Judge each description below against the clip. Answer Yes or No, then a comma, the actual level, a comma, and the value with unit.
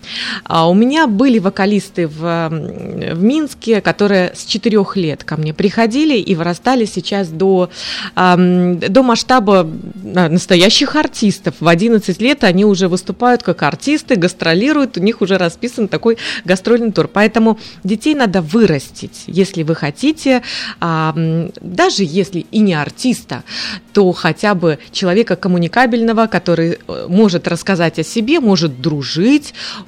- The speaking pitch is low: No, high, 195 Hz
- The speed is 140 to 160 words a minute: No, average, 125 wpm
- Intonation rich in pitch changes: No, average, 4.9 semitones